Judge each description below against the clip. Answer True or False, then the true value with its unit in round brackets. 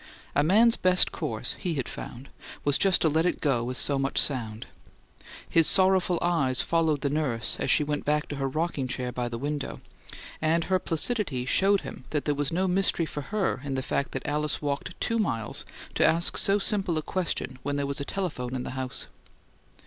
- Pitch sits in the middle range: True (150 Hz)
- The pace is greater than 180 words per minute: True (205 wpm)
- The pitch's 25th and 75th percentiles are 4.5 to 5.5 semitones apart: True (4.9 semitones)